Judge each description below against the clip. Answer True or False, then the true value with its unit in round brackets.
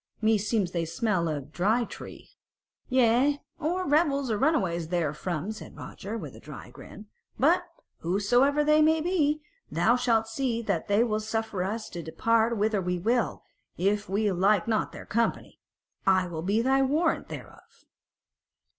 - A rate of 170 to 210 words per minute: False (155 wpm)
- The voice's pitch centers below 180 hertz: False (220 Hz)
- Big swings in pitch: True (5.8 semitones)